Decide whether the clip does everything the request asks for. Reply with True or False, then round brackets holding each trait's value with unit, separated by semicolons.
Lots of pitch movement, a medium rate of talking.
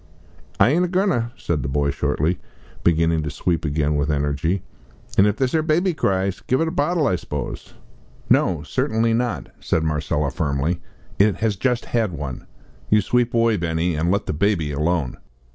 True (7.4 semitones; 180 wpm)